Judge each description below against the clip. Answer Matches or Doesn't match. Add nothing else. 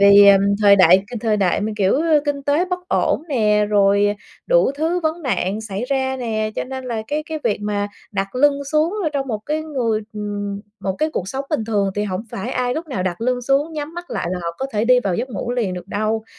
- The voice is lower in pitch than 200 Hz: Doesn't match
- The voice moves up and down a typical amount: Doesn't match